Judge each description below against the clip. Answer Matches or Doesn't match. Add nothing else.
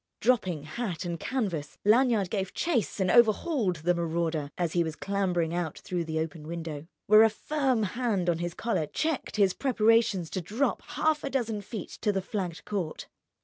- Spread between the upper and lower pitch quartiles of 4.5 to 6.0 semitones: Matches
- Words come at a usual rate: Matches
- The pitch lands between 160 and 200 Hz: Matches